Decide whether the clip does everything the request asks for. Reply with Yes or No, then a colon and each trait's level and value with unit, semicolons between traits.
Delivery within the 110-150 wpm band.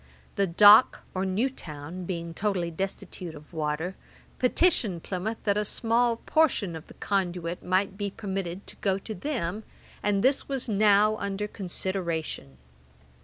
Yes: average, 145 wpm